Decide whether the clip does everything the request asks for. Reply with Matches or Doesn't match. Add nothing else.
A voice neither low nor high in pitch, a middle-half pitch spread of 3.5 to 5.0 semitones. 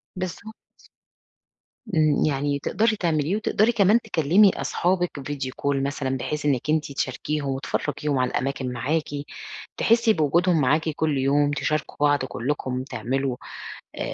Matches